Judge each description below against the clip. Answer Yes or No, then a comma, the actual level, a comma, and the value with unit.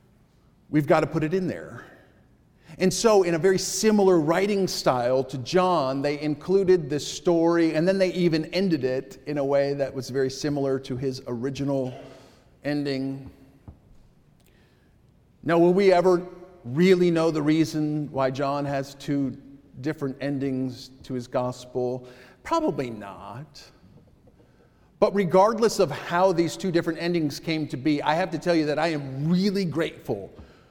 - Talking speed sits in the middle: Yes, average, 150 wpm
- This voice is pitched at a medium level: Yes, medium, 155 Hz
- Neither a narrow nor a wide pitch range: Yes, average, 4.8 semitones